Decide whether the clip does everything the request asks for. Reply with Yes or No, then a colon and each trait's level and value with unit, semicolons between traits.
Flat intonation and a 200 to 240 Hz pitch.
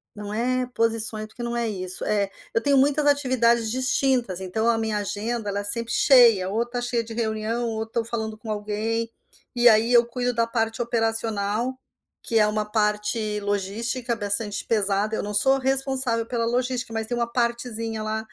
Yes: narrow, 2.1 semitones; high, 225 Hz